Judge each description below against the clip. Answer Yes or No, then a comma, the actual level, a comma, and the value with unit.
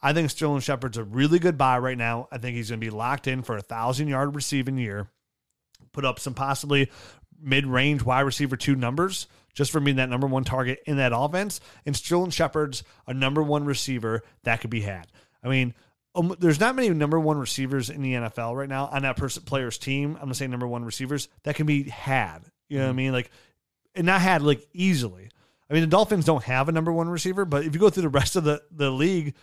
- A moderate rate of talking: No, fast, 240 wpm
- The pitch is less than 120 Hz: No, low, 135 Hz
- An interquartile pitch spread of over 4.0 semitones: No, average, 3.4 semitones